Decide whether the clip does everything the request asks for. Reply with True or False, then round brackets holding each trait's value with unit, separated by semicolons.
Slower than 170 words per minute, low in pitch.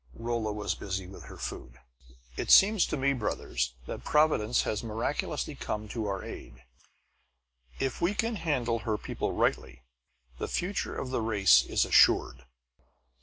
True (150 wpm; 115 Hz)